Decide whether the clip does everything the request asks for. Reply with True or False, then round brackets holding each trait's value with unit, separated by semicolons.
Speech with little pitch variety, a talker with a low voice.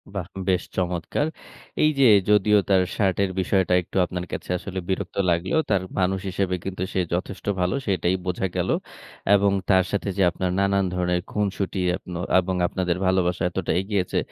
True (1.6 semitones; 95 Hz)